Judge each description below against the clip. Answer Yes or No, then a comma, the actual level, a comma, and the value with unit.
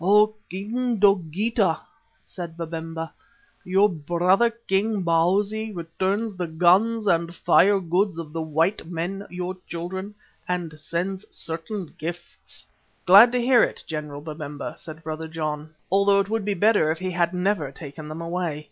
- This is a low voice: No, medium, 180 Hz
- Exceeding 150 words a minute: No, average, 145 wpm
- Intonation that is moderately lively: Yes, average, 3.6 semitones